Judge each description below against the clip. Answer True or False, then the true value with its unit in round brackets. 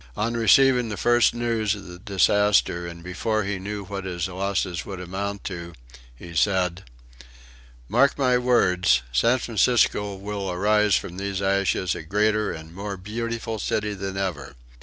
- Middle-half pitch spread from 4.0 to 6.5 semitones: False (2.9 semitones)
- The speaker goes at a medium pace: True (155 wpm)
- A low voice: True (100 Hz)